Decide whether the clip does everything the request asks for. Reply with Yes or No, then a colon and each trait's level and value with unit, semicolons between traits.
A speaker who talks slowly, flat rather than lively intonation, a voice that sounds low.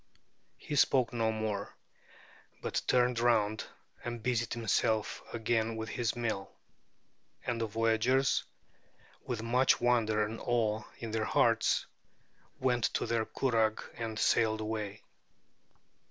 Yes: slow, 120 wpm; narrow, 1.7 semitones; low, 115 Hz